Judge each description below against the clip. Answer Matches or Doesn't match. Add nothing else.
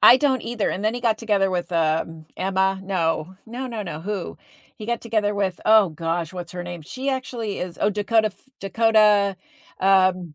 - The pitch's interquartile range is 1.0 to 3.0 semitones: Doesn't match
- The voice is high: Matches